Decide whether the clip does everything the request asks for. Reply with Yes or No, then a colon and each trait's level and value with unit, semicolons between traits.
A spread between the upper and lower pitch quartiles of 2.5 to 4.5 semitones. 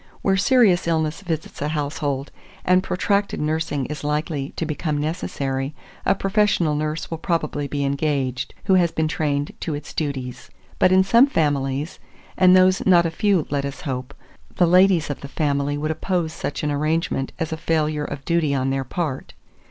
Yes: average, 3.5 semitones